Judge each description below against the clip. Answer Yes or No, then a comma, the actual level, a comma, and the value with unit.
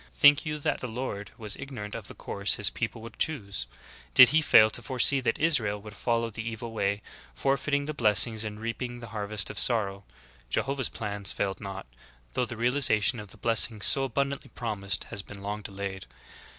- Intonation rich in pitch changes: No, average, 3.9 semitones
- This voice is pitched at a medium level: No, low, 115 Hz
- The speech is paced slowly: No, average, 190 wpm